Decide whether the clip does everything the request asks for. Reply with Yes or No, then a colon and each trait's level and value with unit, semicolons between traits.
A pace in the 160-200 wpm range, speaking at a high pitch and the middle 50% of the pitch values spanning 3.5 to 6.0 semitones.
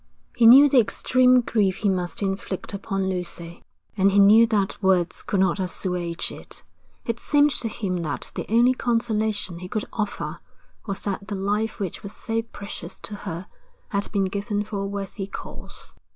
No: average, 175 wpm; high, 200 Hz; average, 2.9 semitones